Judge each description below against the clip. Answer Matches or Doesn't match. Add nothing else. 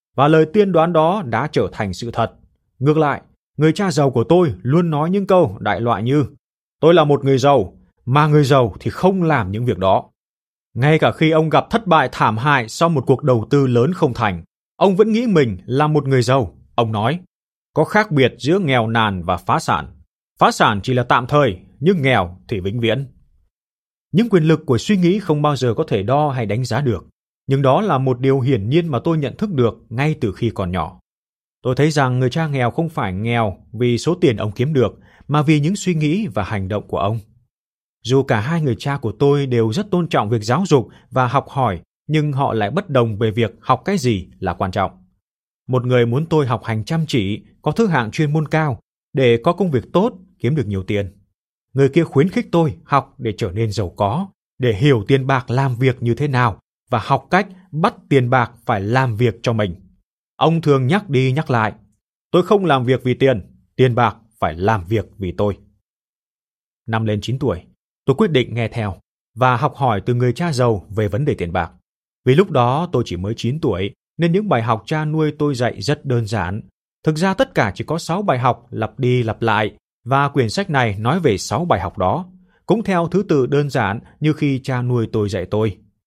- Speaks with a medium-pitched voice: Doesn't match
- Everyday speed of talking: Matches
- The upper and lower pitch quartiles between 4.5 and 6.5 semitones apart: Matches